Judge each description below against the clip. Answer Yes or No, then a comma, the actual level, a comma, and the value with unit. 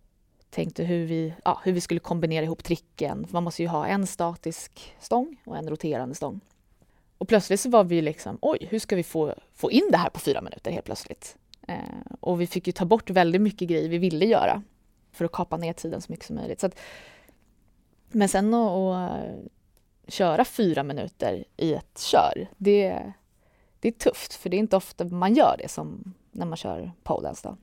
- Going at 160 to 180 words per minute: No, average, 200 wpm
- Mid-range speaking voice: Yes, medium, 180 Hz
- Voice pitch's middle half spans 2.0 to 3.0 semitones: No, average, 3.8 semitones